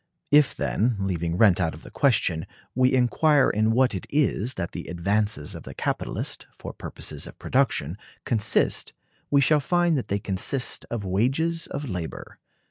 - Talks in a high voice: No, low, 110 Hz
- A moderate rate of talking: Yes, average, 165 wpm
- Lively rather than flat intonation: Yes, wide, 6.7 semitones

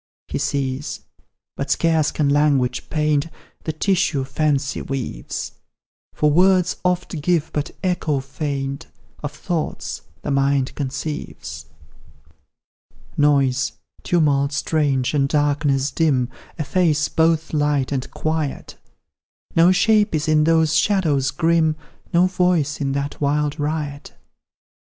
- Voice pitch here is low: No, medium, 150 Hz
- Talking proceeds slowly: Yes, slow, 115 wpm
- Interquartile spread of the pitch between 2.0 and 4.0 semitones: Yes, narrow, 2.6 semitones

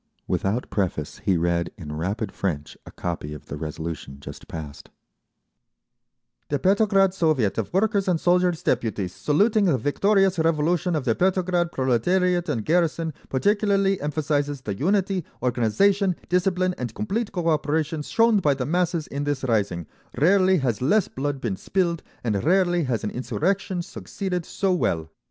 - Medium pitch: Yes, medium, 155 Hz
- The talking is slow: No, average, 145 wpm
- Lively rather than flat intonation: Yes, wide, 8.4 semitones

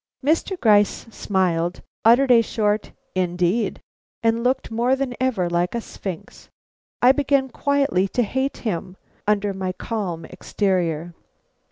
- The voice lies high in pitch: Yes, high, 210 Hz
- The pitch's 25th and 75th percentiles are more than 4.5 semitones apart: Yes, wide, 5.5 semitones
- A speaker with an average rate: No, slow, 130 wpm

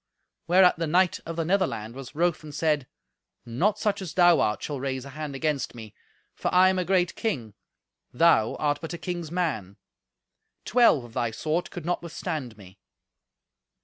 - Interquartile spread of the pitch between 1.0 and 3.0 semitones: No, wide, 5.5 semitones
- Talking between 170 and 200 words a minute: Yes, average, 180 wpm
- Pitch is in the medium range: Yes, medium, 155 Hz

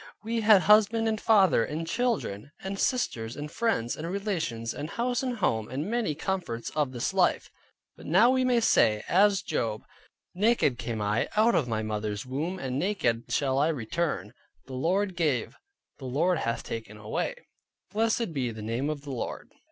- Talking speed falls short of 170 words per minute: No, average, 175 wpm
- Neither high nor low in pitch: Yes, medium, 155 Hz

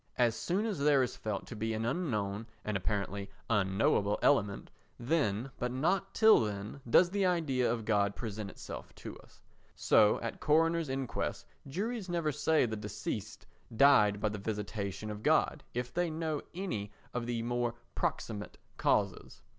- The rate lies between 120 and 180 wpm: Yes, average, 155 wpm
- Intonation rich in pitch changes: Yes, wide, 6.8 semitones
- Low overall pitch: Yes, low, 115 Hz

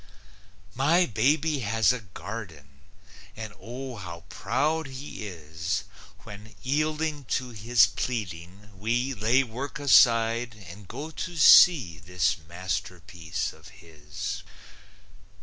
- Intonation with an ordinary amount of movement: No, wide, 6.3 semitones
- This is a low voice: Yes, low, 110 Hz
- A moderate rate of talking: No, slow, 110 wpm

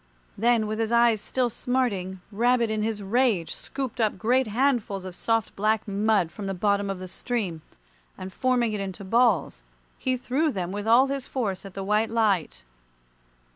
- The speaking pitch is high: Yes, high, 215 Hz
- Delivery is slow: No, average, 175 wpm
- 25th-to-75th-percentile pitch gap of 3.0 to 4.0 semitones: Yes, average, 3.7 semitones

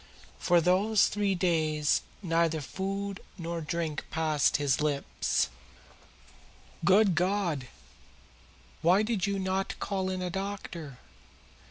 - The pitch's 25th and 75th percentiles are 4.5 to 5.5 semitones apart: No, average, 3.5 semitones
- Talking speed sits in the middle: No, slow, 115 wpm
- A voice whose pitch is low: No, medium, 180 Hz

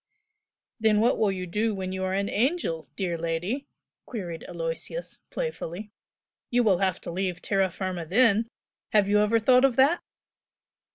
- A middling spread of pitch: Yes, average, 4.0 semitones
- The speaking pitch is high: Yes, high, 200 Hz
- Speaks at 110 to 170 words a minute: Yes, average, 160 wpm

